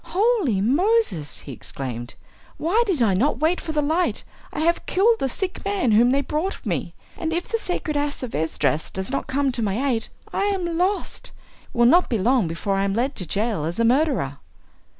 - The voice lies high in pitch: Yes, very high, 275 Hz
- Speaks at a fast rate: Yes, fast, 210 wpm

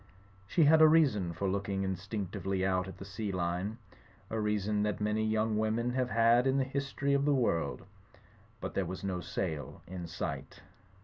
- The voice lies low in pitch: Yes, low, 105 Hz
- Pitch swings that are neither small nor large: Yes, average, 4.0 semitones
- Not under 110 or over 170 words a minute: No, average, 185 wpm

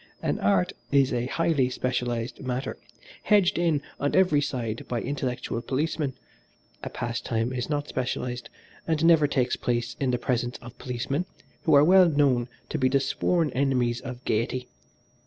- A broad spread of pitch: No, average, 3.1 semitones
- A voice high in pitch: No, low, 130 Hz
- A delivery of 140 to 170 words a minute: Yes, average, 155 wpm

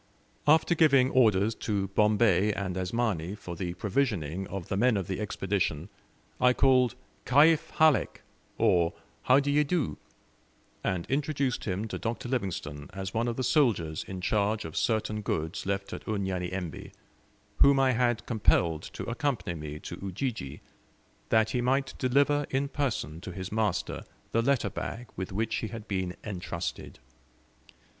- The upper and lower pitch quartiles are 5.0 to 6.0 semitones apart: Yes, wide, 5.4 semitones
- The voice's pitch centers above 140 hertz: No, low, 105 Hz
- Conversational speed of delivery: Yes, average, 150 wpm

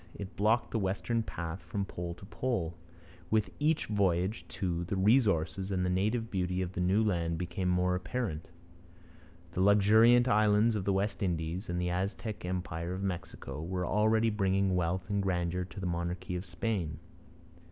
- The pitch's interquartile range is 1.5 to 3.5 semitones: Yes, average, 2.9 semitones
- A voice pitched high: No, very low, 95 Hz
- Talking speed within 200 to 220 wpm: No, average, 170 wpm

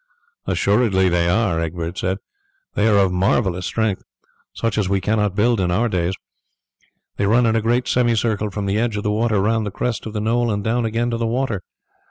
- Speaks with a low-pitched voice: Yes, low, 105 Hz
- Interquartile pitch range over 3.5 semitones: No, average, 3.1 semitones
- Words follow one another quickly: Yes, fast, 210 wpm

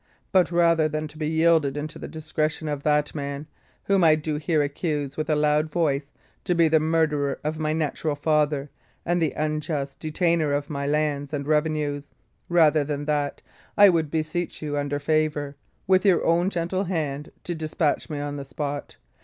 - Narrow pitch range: Yes, narrow, 1.8 semitones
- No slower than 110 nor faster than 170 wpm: No, average, 180 wpm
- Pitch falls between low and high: Yes, medium, 155 Hz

